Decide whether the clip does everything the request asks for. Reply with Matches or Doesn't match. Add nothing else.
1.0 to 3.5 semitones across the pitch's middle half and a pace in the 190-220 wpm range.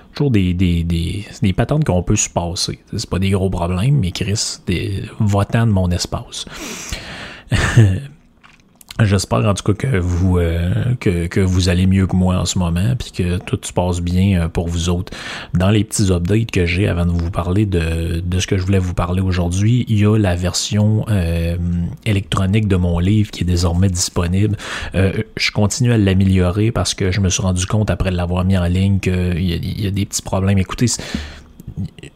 Matches